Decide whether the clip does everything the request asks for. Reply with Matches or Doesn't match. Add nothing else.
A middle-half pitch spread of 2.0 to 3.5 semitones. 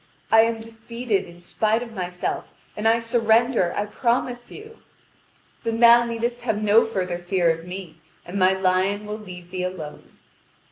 Doesn't match